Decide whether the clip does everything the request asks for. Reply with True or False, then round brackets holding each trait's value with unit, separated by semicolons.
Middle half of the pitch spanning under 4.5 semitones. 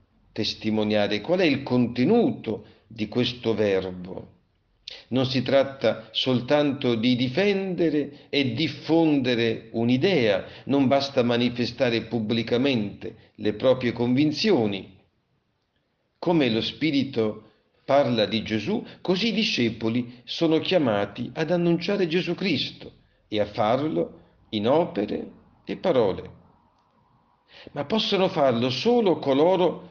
False (4.9 semitones)